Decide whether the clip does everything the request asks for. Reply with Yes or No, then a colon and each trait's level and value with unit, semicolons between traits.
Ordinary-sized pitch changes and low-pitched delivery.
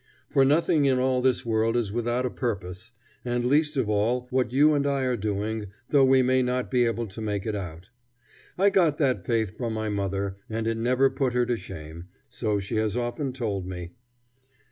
Yes: average, 3.8 semitones; low, 120 Hz